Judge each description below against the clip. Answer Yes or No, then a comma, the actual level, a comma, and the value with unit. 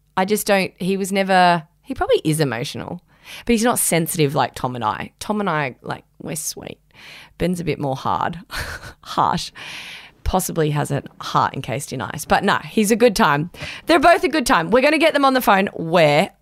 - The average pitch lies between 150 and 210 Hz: Yes, medium, 185 Hz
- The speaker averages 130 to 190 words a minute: No, fast, 205 wpm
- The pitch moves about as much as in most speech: No, wide, 7.8 semitones